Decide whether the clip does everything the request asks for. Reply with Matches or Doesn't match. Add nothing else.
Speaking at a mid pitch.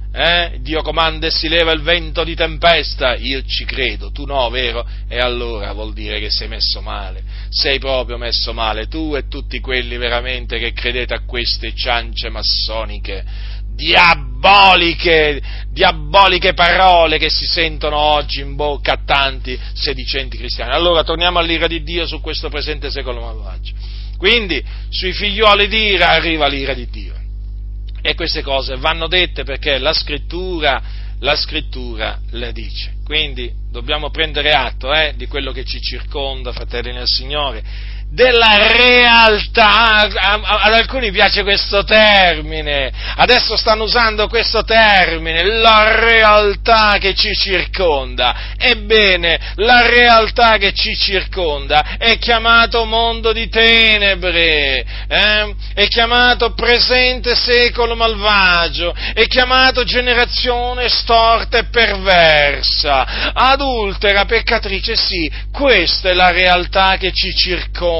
Matches